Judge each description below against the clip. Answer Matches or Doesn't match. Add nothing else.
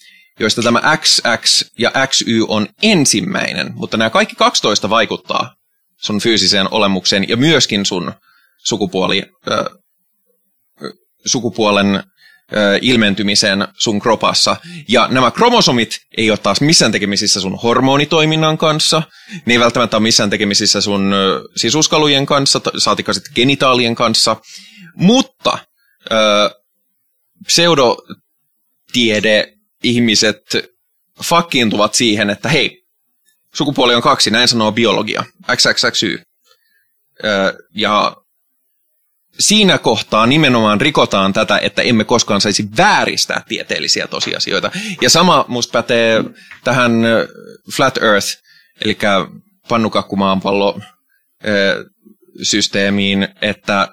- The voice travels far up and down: Matches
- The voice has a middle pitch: Doesn't match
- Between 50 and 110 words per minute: Matches